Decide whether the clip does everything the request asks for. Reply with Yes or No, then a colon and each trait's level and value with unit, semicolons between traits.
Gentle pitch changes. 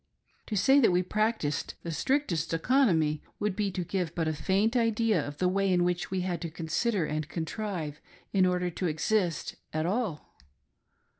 No: average, 4.6 semitones